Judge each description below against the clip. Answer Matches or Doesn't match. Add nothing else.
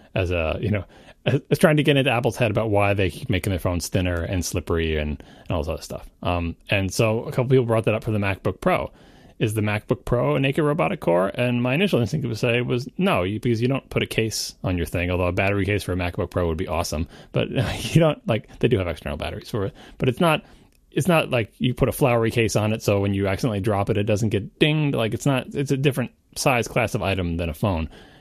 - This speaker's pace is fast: Matches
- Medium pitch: Doesn't match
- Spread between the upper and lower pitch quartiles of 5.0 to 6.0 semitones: Matches